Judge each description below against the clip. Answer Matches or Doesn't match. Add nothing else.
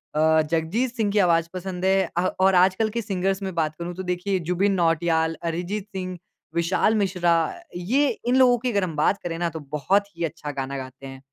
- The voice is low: Doesn't match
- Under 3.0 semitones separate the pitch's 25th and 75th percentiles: Doesn't match